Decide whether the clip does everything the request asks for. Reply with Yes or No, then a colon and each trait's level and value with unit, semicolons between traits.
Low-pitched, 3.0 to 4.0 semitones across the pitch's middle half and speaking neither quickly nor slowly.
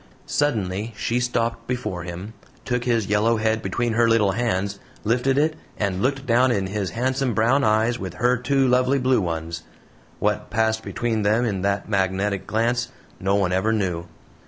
Yes: low, 110 Hz; average, 3.7 semitones; average, 170 wpm